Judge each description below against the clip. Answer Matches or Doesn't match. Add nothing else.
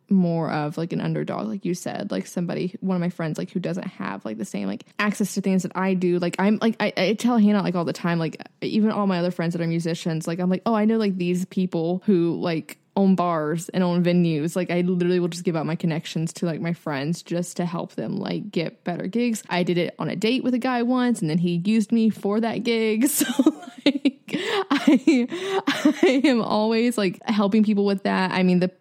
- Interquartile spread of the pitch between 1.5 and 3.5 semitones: Doesn't match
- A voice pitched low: Doesn't match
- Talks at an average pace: Doesn't match